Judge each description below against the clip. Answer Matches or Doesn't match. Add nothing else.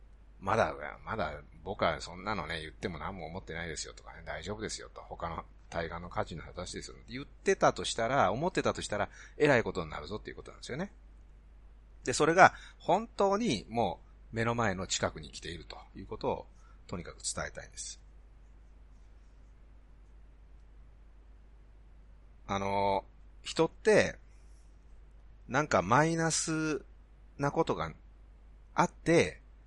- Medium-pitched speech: Doesn't match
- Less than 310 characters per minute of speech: Matches